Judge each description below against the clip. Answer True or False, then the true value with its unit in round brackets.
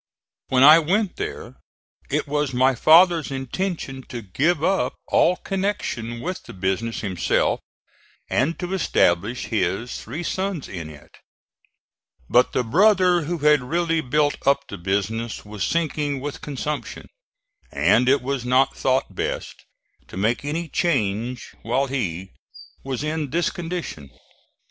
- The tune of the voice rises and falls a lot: True (6.2 semitones)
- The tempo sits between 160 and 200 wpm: False (135 wpm)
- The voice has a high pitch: False (135 Hz)